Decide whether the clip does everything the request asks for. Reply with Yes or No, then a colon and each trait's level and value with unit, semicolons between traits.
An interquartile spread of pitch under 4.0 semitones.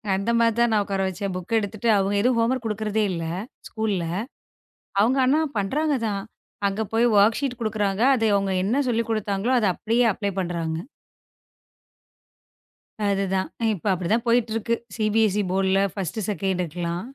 Yes: average, 2.9 semitones